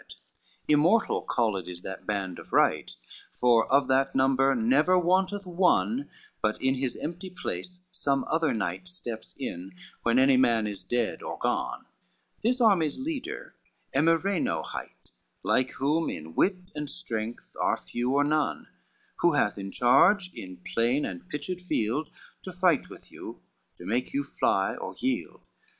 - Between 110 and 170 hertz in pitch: Yes, low, 135 Hz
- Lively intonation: Yes, wide, 8.0 semitones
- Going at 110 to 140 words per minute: No, average, 155 wpm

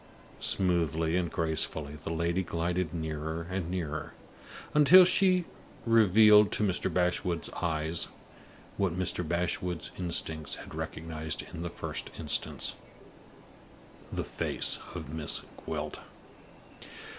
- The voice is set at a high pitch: No, very low, 85 Hz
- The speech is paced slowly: Yes, slow, 110 wpm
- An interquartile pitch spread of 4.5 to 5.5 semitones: No, narrow, 2.5 semitones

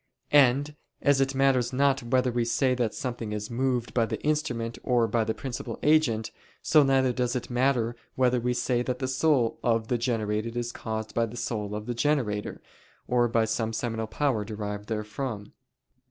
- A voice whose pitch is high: No, low, 120 Hz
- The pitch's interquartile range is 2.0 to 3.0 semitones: Yes, average, 2.7 semitones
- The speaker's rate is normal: Yes, average, 185 wpm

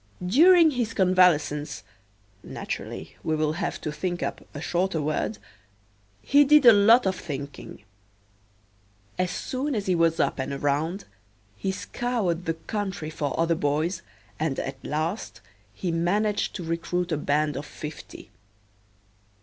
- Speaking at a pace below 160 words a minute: Yes, average, 140 wpm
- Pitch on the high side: No, medium, 170 Hz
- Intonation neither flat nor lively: Yes, average, 4.8 semitones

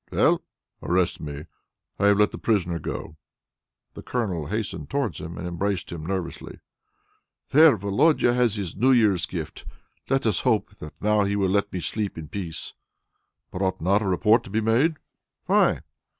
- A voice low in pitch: Yes, low, 100 Hz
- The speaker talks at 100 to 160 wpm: No, average, 170 wpm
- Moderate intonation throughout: Yes, average, 4.1 semitones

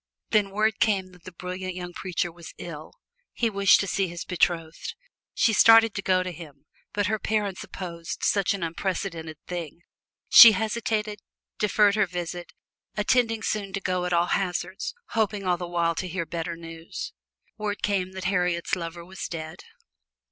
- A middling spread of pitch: Yes, average, 3.1 semitones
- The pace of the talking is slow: No, average, 170 wpm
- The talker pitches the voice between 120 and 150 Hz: No, medium, 185 Hz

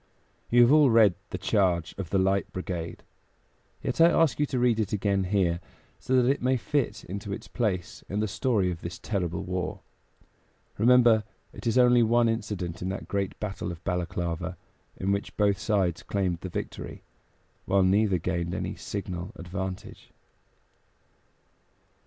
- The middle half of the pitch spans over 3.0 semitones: Yes, average, 4.0 semitones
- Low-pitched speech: Yes, low, 100 Hz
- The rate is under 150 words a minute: No, average, 160 wpm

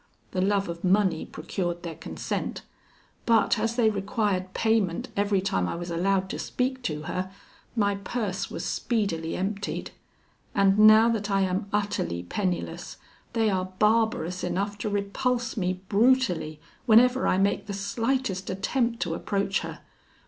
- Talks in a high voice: Yes, high, 200 Hz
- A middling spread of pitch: Yes, average, 3.1 semitones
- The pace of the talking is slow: No, average, 150 wpm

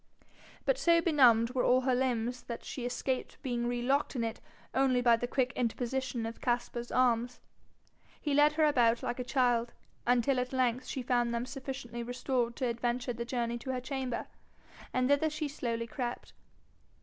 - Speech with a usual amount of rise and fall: No, narrow, 1.8 semitones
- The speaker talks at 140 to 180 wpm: Yes, average, 175 wpm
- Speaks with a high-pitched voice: Yes, very high, 250 Hz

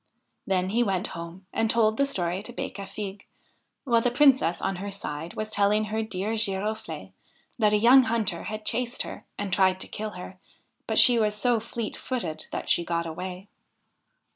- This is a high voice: Yes, high, 210 Hz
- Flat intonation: No, average, 3.3 semitones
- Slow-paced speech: No, average, 180 wpm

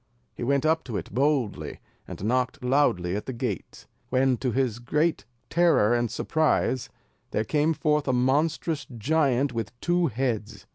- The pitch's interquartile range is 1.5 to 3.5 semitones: No, average, 4.4 semitones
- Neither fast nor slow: Yes, average, 155 wpm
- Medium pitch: No, low, 130 Hz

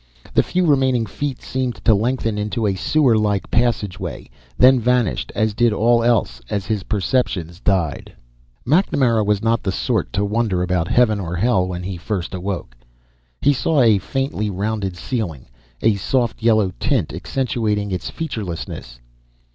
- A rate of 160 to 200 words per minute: No, average, 150 wpm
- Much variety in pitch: No, average, 4.2 semitones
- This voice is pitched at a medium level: No, low, 110 Hz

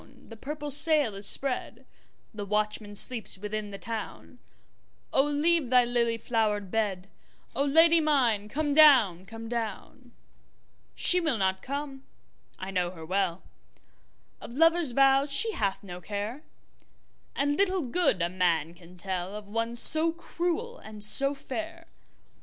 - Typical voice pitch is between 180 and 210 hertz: No, high, 230 Hz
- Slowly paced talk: Yes, slow, 125 wpm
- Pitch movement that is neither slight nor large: No, wide, 6.6 semitones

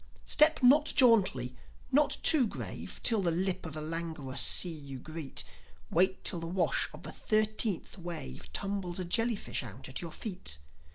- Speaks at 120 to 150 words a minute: No, average, 165 wpm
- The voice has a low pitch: No, medium, 175 Hz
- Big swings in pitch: Yes, wide, 5.8 semitones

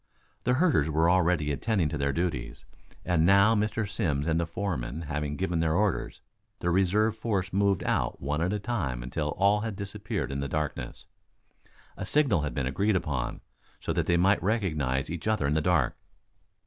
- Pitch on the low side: Yes, very low, 85 Hz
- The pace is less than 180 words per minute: No, average, 185 wpm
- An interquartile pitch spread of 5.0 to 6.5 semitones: Yes, average, 5.3 semitones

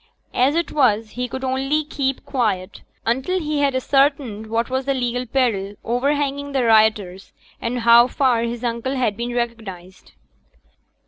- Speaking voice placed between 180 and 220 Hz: No, high, 245 Hz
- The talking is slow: No, average, 150 wpm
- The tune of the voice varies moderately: Yes, average, 3.1 semitones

